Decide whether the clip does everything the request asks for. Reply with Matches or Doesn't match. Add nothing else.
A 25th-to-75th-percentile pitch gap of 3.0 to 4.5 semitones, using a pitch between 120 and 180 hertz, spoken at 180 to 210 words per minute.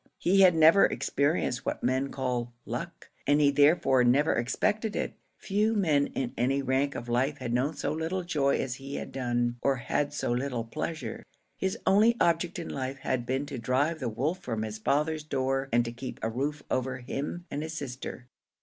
Matches